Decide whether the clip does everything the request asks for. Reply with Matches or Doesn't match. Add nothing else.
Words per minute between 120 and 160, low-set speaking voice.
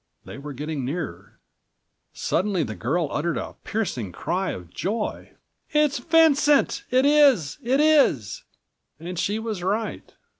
Doesn't match